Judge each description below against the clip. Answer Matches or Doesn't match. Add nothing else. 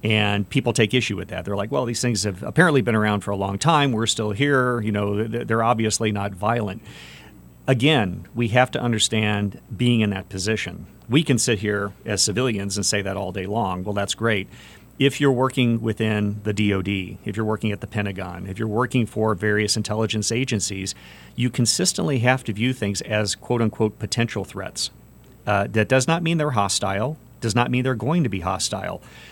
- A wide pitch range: Doesn't match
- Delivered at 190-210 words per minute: Matches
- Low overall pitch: Matches